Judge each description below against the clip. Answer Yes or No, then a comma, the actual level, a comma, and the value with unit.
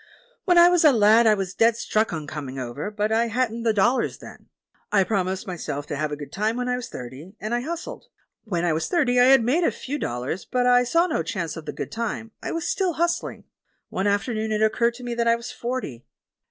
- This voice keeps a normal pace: No, fast, 245 wpm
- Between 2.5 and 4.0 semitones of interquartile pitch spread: No, average, 5.3 semitones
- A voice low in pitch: No, high, 225 Hz